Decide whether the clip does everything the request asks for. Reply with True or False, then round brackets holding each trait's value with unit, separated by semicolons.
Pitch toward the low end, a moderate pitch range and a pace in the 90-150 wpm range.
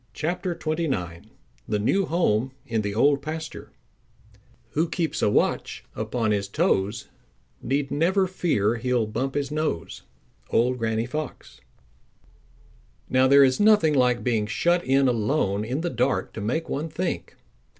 False (130 Hz; 6.1 semitones; 140 wpm)